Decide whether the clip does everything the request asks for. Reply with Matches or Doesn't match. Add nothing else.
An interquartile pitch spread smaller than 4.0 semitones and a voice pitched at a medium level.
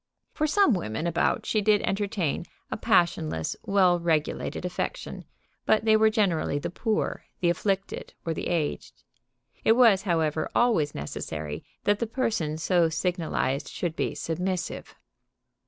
Doesn't match